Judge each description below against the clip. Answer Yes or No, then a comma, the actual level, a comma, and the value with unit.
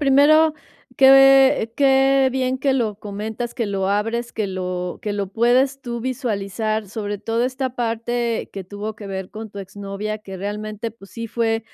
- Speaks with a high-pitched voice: Yes, high, 225 Hz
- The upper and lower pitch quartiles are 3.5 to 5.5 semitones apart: Yes, average, 4.1 semitones